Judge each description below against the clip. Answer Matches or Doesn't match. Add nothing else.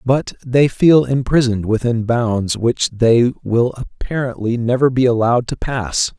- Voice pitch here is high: Doesn't match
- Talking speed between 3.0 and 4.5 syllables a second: Matches